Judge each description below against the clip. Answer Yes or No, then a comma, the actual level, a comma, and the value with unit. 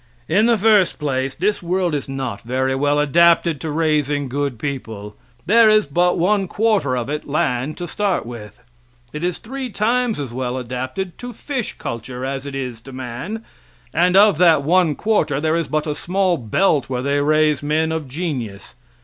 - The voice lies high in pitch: No, medium, 150 Hz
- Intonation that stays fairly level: No, wide, 5.6 semitones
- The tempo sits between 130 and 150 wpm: No, average, 185 wpm